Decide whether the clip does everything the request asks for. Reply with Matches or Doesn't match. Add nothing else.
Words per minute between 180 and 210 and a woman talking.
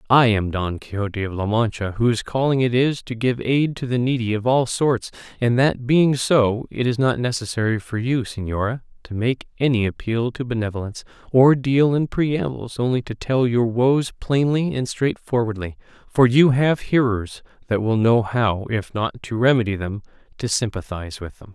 Doesn't match